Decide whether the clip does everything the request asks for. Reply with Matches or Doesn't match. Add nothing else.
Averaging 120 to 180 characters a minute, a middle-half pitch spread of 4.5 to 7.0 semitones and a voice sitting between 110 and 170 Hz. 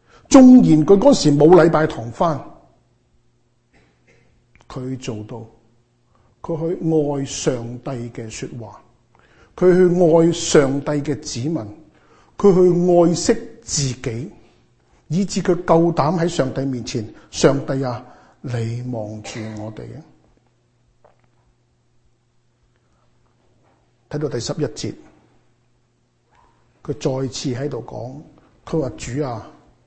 Matches